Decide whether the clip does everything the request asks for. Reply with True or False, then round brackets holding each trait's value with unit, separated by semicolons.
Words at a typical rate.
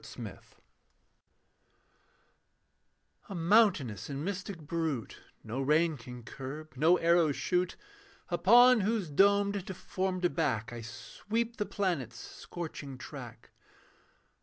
False (100 wpm)